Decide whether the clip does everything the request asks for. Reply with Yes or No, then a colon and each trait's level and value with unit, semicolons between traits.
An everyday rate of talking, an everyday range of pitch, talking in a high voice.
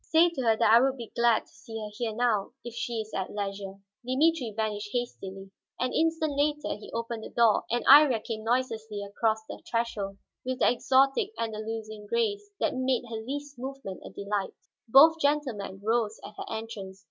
Yes: average, 185 wpm; average, 3.5 semitones; high, 230 Hz